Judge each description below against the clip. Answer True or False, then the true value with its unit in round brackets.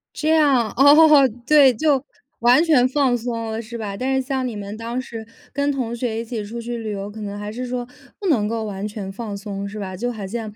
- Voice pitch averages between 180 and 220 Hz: False (230 Hz)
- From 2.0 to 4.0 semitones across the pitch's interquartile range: True (3.4 semitones)